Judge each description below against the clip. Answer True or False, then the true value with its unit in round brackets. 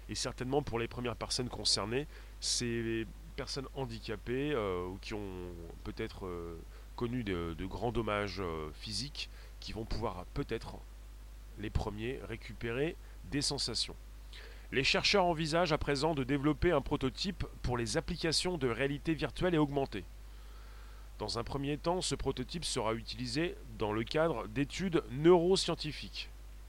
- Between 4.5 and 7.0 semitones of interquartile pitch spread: True (5.2 semitones)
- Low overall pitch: True (120 Hz)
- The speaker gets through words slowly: True (140 wpm)